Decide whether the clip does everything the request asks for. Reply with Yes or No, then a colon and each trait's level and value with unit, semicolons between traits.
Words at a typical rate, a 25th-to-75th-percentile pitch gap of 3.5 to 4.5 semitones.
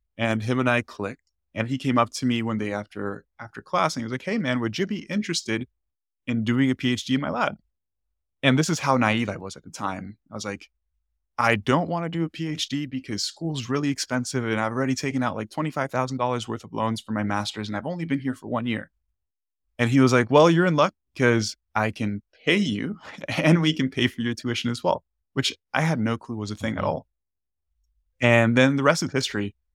No: fast, 235 wpm; average, 4.2 semitones